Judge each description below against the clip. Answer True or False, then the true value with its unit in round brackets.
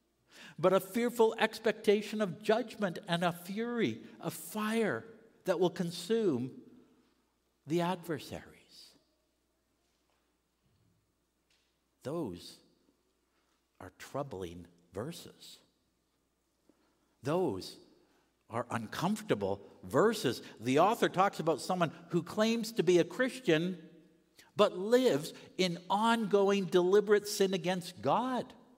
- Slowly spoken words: True (90 wpm)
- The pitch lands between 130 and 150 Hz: False (190 Hz)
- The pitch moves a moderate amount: True (4.5 semitones)